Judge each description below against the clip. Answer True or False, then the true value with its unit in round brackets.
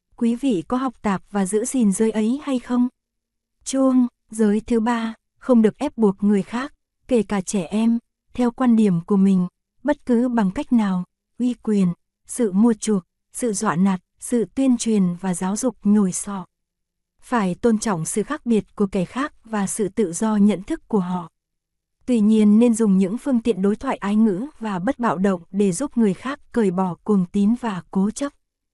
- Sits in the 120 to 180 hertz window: False (220 Hz)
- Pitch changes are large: False (3.5 semitones)